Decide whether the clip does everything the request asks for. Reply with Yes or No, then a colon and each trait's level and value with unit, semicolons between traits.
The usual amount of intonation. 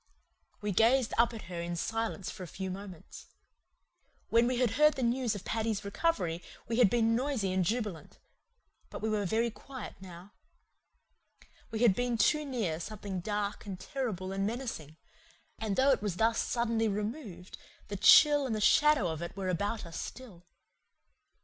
Yes: average, 4.2 semitones